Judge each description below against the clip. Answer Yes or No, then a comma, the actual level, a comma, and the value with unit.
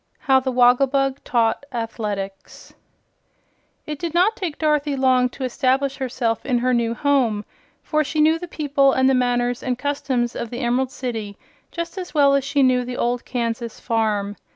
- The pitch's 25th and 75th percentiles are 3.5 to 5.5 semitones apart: No, average, 2.9 semitones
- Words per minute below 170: No, average, 175 wpm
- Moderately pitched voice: No, very high, 255 Hz